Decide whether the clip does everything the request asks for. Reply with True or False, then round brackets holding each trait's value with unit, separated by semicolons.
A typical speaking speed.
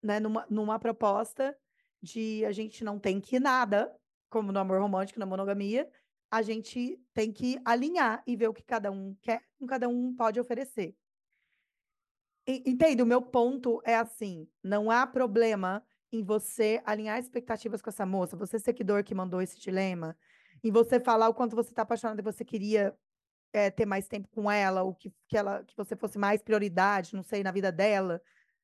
False (190 wpm)